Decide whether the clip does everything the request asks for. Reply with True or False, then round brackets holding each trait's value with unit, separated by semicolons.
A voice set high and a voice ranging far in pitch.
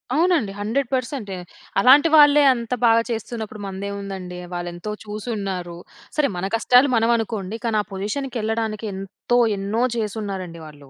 False (215 Hz; 3.7 semitones)